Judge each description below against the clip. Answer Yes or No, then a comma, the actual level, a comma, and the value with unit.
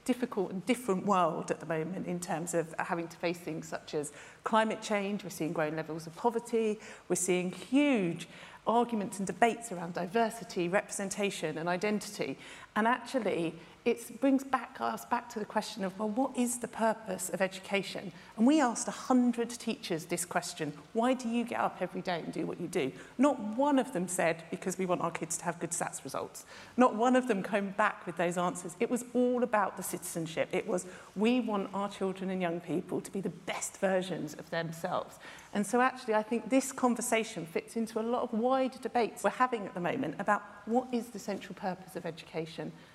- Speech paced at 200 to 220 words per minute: Yes, fast, 205 wpm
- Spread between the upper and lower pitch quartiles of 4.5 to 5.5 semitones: Yes, average, 4.9 semitones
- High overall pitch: Yes, high, 200 Hz